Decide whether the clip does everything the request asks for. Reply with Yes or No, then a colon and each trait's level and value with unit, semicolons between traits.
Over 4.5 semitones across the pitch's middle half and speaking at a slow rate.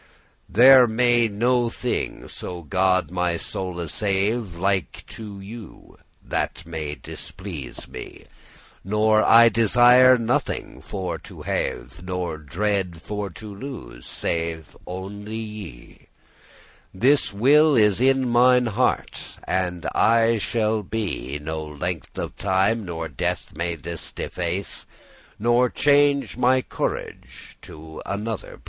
Yes: average, 5.1 semitones; slow, 125 wpm